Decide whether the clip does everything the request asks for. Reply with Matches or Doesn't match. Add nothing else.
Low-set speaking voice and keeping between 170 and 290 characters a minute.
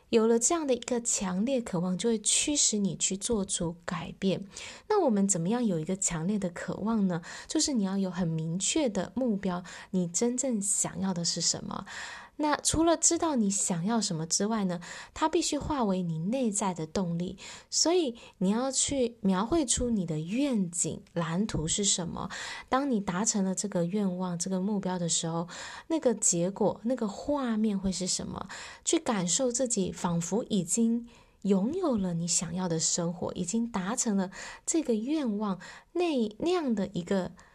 Doesn't match